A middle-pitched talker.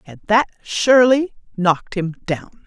No: high, 205 Hz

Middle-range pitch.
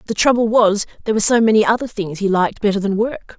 No: high, 215 Hz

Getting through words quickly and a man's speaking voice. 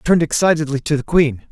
Yes: fast, 235 wpm; male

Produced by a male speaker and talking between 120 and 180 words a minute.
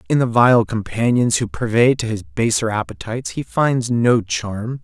Yes: male; average, 175 wpm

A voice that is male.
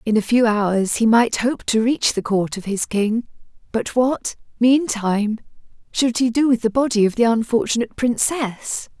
No: female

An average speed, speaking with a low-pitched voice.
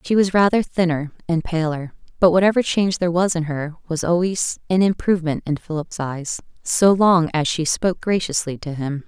No: average, 185 wpm; medium, 170 Hz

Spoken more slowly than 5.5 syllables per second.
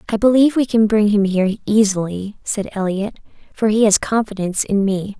No: 5.6 syllables/s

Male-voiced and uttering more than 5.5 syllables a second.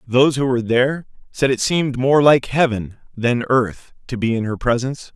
No: male; 5.4 syllables/s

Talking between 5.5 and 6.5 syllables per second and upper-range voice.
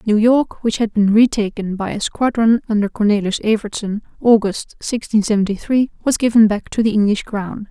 No: 5.2 syllables/s; high, 215 Hz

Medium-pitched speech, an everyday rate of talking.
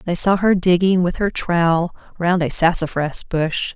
Yes: medium, 175 Hz; average, 175 wpm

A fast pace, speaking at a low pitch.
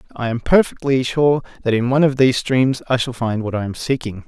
Yes: fast, 240 wpm; low, 125 Hz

